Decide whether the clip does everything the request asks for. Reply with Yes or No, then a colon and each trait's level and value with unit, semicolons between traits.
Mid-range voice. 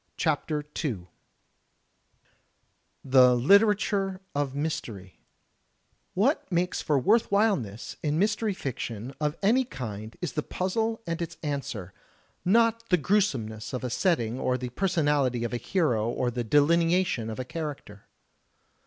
Yes: medium, 150 Hz